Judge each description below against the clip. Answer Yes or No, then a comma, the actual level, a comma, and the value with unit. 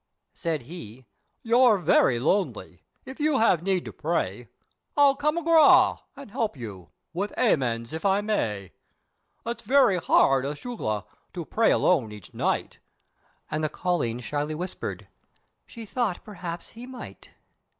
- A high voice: No, medium, 180 Hz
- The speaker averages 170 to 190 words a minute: No, average, 140 wpm